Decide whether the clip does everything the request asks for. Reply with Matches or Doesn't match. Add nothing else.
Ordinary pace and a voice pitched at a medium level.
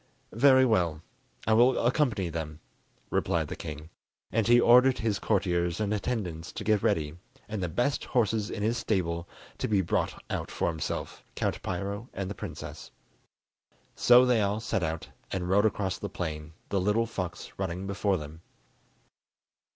Doesn't match